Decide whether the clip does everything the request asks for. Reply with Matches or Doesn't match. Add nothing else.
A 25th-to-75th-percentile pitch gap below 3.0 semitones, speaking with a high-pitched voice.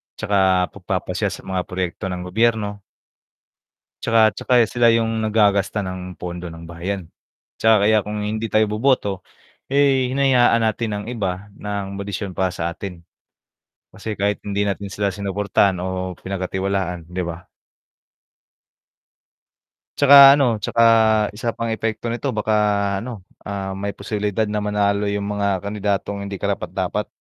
Doesn't match